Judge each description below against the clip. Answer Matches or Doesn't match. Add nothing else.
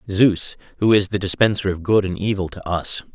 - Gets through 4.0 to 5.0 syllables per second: Doesn't match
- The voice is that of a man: Matches